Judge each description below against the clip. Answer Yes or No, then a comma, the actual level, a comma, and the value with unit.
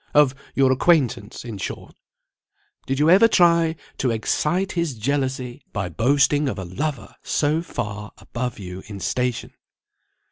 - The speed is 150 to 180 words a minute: No, average, 140 wpm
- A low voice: Yes, low, 130 Hz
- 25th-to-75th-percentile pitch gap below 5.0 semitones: No, average, 5.3 semitones